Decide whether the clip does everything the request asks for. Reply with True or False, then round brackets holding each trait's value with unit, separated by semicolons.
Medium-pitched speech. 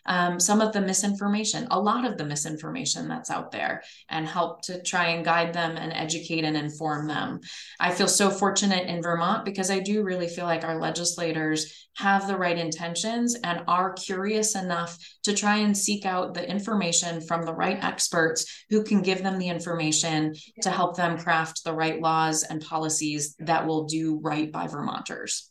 True (170 Hz)